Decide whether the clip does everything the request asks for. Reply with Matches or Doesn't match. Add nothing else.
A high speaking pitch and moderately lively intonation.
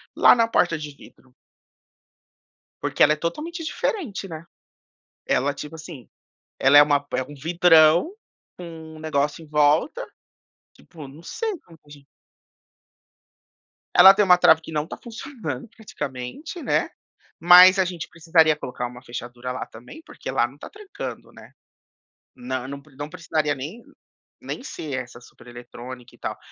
Doesn't match